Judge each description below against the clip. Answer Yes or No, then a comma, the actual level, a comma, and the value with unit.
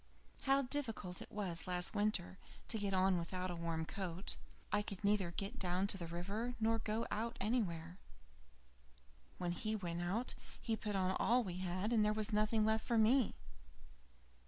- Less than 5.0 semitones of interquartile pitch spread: Yes, average, 3.6 semitones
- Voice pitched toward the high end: Yes, high, 200 Hz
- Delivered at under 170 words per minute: No, average, 175 wpm